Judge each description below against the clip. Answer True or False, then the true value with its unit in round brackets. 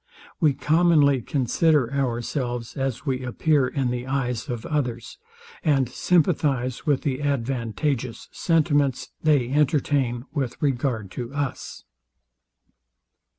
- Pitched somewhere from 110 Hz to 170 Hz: True (135 Hz)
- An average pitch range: True (3.1 semitones)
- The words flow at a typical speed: False (110 wpm)